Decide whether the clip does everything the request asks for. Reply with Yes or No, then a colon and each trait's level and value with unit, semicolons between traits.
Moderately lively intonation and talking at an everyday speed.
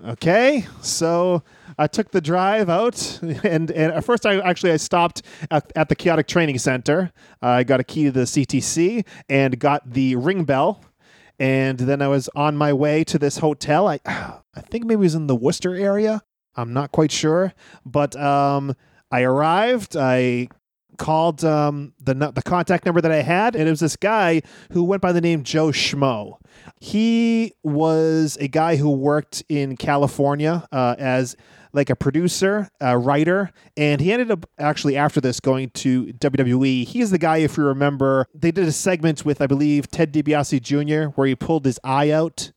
Yes: average, 3.7 semitones; average, 185 wpm